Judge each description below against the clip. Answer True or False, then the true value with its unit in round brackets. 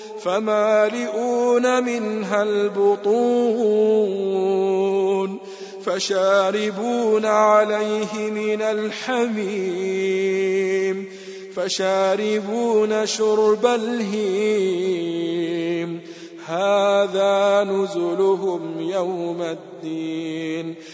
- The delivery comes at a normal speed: False (40 wpm)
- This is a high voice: True (195 Hz)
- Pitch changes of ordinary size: False (2.1 semitones)